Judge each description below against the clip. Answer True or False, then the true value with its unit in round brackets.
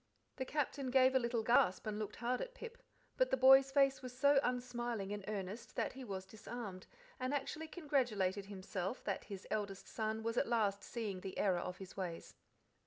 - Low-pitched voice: False (230 Hz)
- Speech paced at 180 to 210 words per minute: True (190 wpm)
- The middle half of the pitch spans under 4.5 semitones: False (4.8 semitones)